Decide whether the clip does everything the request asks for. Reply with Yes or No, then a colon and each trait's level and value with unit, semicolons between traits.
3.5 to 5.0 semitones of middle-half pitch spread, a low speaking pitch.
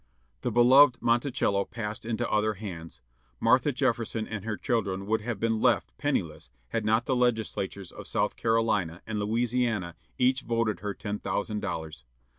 No: average, 2.7 semitones; low, 110 Hz